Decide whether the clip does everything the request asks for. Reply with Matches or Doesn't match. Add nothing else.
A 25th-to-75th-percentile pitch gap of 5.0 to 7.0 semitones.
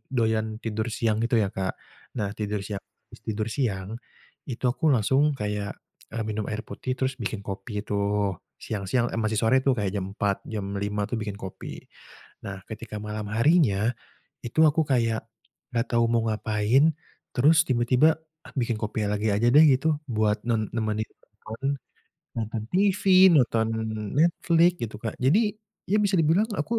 Doesn't match